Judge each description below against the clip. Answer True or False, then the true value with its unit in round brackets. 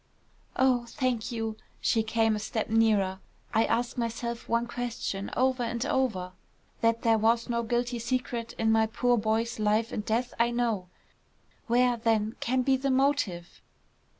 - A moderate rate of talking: True (160 wpm)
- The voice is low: False (230 Hz)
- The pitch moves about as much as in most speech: False (1.7 semitones)